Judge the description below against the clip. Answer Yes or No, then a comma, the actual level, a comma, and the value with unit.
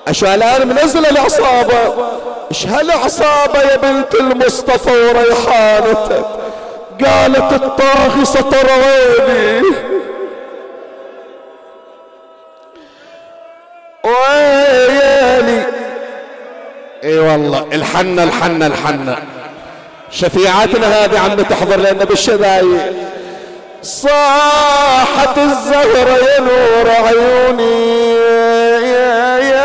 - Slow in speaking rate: Yes, slow, 60 wpm